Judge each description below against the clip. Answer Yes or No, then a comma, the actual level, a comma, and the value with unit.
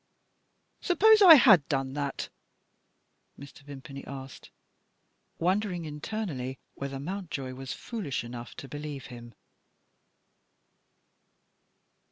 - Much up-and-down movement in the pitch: Yes, wide, 5.9 semitones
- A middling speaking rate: No, slow, 90 wpm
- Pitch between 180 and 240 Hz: No, medium, 140 Hz